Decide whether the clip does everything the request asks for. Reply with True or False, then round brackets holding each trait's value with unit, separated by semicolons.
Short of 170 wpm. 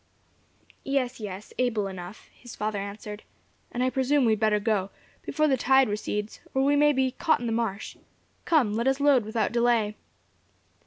False (175 wpm)